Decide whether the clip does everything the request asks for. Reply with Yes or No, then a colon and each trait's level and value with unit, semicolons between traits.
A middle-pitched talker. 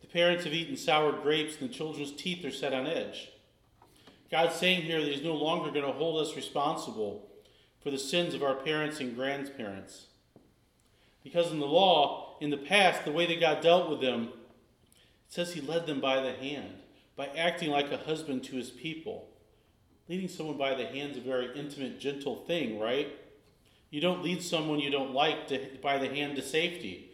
Yes: medium, 150 Hz